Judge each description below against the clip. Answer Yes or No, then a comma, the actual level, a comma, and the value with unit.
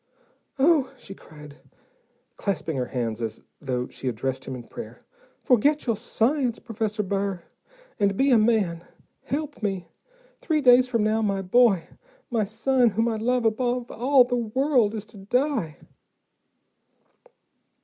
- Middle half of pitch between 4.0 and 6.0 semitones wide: Yes, average, 4.7 semitones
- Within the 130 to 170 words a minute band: Yes, average, 140 wpm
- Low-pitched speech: No, high, 220 Hz